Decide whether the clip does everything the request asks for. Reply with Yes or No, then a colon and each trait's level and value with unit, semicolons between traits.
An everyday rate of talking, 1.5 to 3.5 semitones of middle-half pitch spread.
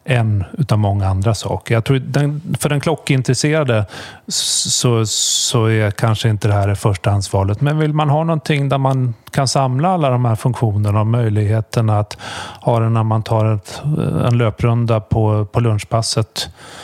No: average, 165 wpm; average, 4.2 semitones